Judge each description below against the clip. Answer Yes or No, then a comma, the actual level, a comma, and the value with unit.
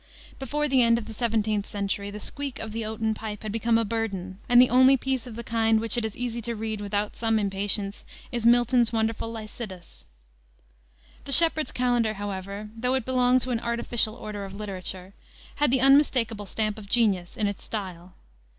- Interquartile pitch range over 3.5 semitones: No, average, 2.8 semitones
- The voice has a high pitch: Yes, high, 225 Hz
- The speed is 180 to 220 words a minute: Yes, average, 190 wpm